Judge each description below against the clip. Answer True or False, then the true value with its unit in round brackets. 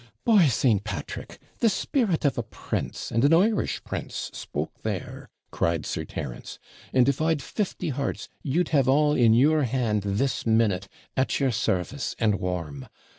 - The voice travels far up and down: True (6.3 semitones)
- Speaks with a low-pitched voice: True (130 Hz)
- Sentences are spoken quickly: False (160 wpm)